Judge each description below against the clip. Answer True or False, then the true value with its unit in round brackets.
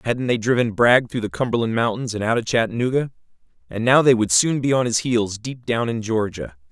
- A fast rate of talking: True (225 wpm)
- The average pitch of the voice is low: True (115 Hz)